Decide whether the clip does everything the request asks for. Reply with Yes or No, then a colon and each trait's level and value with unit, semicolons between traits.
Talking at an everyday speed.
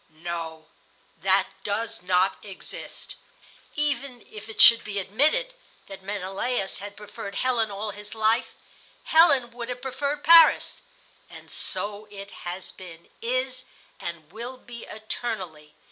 No: slow, 130 wpm